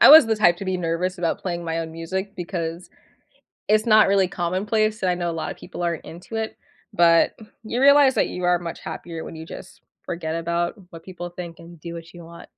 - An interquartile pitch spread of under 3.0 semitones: Yes, narrow, 2.5 semitones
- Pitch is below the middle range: No, medium, 175 Hz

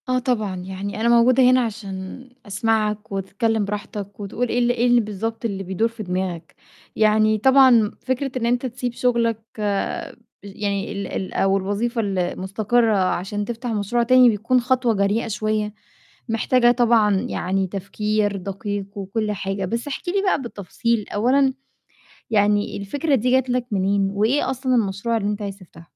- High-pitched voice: Yes, high, 215 Hz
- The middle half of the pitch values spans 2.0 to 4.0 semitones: Yes, average, 3.3 semitones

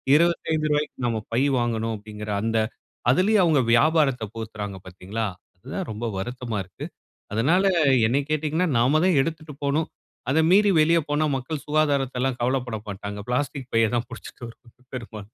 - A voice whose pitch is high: No, low, 130 Hz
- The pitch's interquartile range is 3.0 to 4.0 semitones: No, average, 5.2 semitones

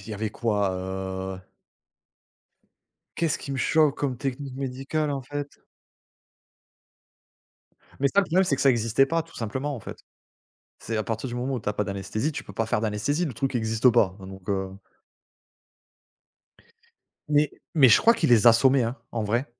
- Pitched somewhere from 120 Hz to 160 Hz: Yes, low, 125 Hz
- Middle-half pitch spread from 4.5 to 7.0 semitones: Yes, average, 4.8 semitones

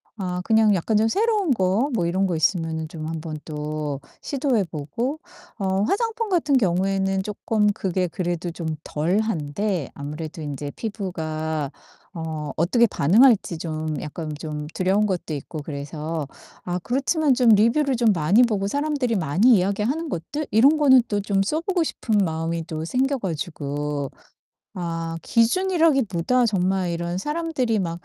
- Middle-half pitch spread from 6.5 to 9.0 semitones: Yes, wide, 6.8 semitones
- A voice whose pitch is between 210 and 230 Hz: No, high, 190 Hz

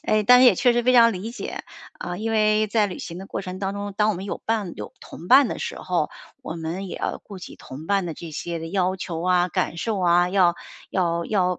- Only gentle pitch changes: No, average, 3.4 semitones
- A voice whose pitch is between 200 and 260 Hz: No, high, 190 Hz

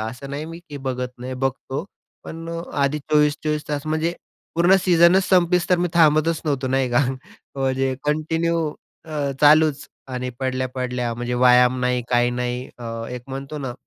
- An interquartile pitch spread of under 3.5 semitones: No, average, 3.8 semitones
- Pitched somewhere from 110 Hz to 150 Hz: Yes, medium, 140 Hz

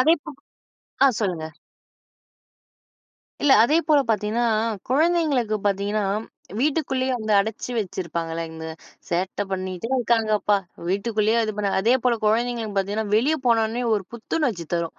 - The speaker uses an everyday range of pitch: Yes, average, 3.9 semitones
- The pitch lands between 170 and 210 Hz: No, high, 220 Hz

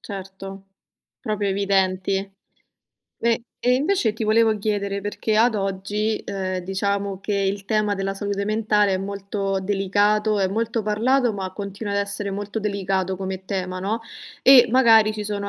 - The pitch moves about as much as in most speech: No, narrow, 1.7 semitones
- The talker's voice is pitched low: No, high, 200 Hz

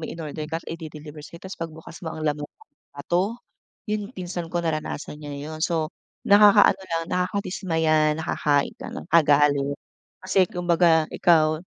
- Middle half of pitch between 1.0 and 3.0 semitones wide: Yes, average, 2.7 semitones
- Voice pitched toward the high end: No, medium, 165 Hz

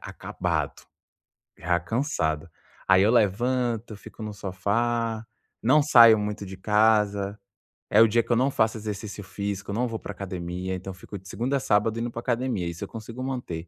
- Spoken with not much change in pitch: No, average, 3.4 semitones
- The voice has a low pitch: Yes, low, 105 Hz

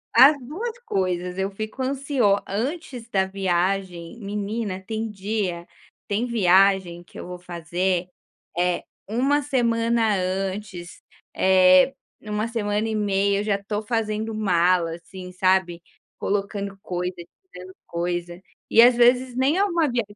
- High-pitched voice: Yes, high, 200 Hz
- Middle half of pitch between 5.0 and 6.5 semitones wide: No, average, 3.9 semitones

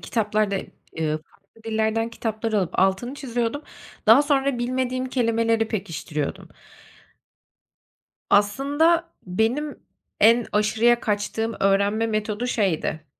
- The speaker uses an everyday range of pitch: Yes, average, 3.1 semitones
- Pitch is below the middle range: No, high, 225 Hz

